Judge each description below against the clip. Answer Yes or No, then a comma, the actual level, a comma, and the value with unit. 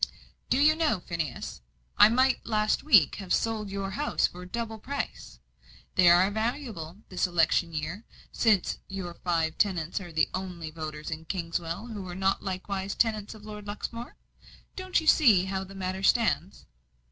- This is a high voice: Yes, high, 195 Hz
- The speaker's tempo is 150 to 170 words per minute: Yes, average, 160 wpm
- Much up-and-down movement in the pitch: No, average, 4.1 semitones